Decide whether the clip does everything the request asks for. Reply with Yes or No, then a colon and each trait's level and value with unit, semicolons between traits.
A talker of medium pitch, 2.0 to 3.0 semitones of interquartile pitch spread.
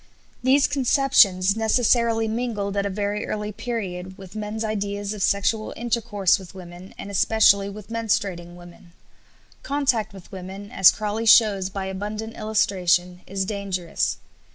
No: high, 205 Hz; narrow, 2.6 semitones